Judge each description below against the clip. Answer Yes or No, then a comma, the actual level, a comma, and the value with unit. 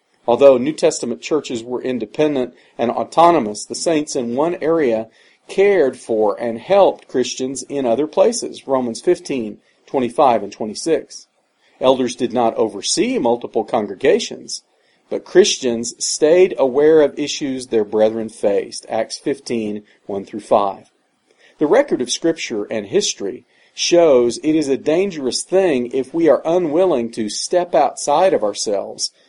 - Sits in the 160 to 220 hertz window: No, low, 135 Hz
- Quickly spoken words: No, slow, 135 wpm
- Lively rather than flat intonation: Yes, wide, 5.7 semitones